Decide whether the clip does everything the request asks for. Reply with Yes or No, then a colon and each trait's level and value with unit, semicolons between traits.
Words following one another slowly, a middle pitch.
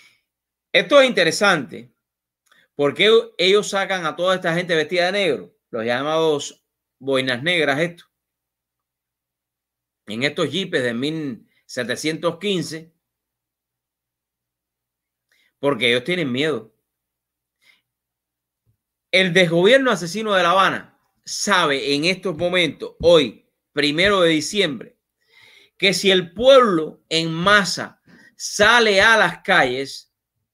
Yes: slow, 100 wpm; medium, 155 Hz